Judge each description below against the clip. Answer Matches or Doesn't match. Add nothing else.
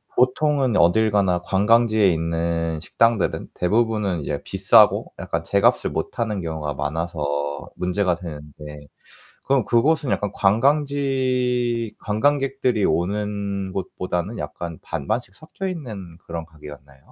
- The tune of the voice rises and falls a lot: Matches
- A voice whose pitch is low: Matches